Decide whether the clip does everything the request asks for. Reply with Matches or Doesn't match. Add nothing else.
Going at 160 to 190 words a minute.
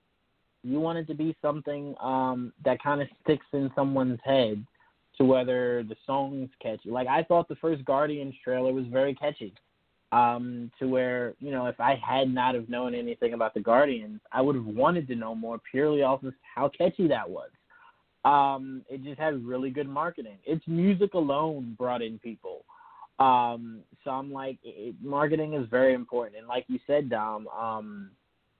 Matches